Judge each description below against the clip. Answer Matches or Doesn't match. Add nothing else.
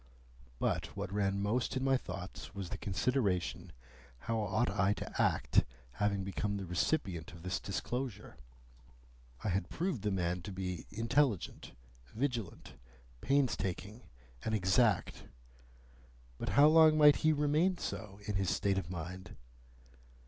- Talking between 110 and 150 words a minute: Matches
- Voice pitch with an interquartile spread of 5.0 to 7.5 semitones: Matches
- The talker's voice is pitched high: Doesn't match